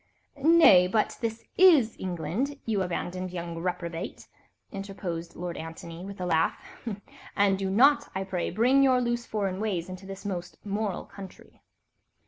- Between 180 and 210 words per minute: No, average, 145 wpm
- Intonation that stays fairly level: No, average, 3.7 semitones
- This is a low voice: No, high, 195 Hz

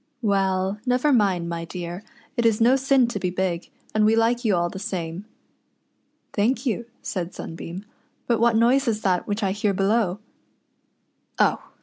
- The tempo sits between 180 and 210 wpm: Yes, average, 190 wpm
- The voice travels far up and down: No, average, 4.1 semitones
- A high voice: Yes, high, 205 Hz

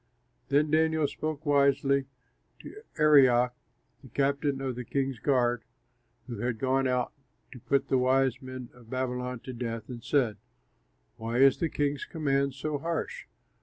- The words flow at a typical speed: Yes, average, 150 wpm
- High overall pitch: No, low, 135 Hz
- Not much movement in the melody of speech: Yes, narrow, 2.2 semitones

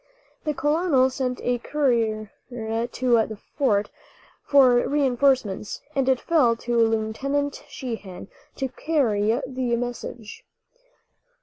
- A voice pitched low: No, high, 245 Hz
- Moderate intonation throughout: Yes, average, 3.5 semitones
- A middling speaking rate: No, slow, 105 wpm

